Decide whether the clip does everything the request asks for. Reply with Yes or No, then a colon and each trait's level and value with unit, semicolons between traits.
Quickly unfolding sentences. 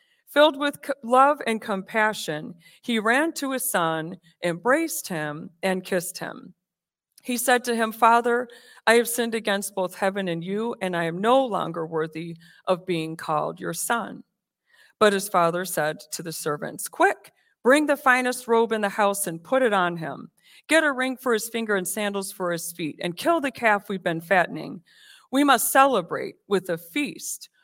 No: average, 180 wpm